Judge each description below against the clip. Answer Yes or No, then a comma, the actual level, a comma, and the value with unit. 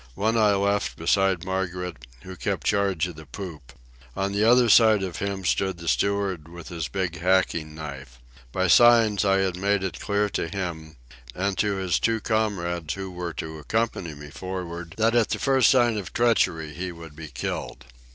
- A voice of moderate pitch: No, very low, 95 Hz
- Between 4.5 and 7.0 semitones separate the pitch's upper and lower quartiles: No, average, 3.5 semitones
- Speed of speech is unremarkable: Yes, average, 185 wpm